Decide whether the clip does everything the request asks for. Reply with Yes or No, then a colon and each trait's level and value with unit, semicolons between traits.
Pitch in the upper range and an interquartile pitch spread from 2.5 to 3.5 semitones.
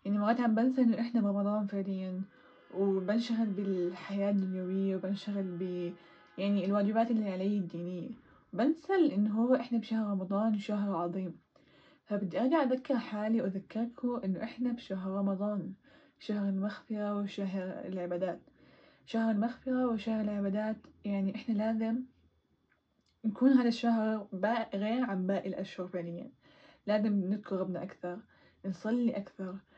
Yes: high, 205 Hz; average, 3.1 semitones